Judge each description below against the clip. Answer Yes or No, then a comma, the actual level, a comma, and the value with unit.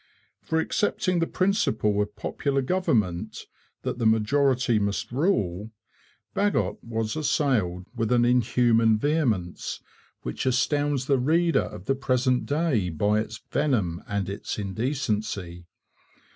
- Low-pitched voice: Yes, low, 120 Hz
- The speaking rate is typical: No, slow, 120 wpm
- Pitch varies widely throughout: Yes, wide, 5.7 semitones